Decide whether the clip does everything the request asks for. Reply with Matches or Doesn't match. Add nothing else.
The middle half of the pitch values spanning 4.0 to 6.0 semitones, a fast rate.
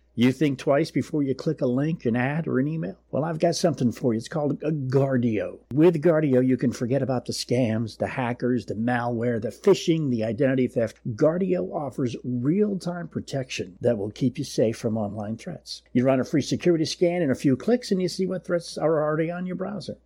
Matches